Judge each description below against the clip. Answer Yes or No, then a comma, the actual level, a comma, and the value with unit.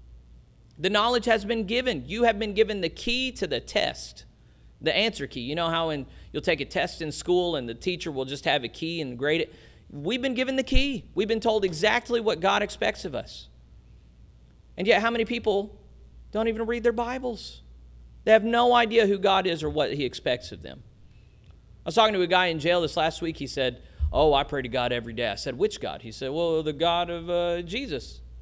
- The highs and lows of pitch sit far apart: Yes, wide, 8.7 semitones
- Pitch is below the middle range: No, medium, 170 Hz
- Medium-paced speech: No, fast, 225 wpm